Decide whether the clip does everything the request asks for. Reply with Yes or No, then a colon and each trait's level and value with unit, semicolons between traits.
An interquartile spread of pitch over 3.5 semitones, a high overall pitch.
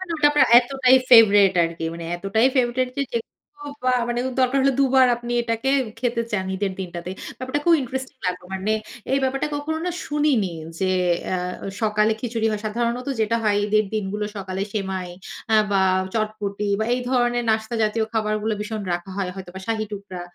Yes: average, 4.2 semitones; high, 220 Hz